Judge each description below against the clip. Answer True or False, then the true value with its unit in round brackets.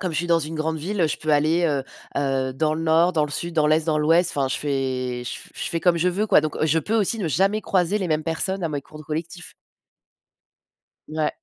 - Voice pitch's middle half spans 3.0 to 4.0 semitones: False (2.6 semitones)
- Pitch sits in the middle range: True (160 Hz)